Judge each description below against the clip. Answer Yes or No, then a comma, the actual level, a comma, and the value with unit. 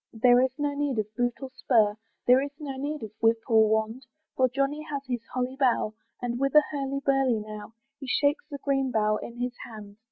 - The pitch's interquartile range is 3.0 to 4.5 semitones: Yes, average, 3.5 semitones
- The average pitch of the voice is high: Yes, very high, 255 Hz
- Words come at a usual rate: No, fast, 215 wpm